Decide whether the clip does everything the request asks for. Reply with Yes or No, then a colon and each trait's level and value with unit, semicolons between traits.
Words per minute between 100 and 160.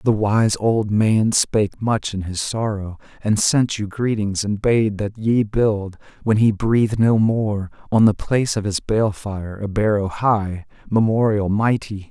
No: average, 170 wpm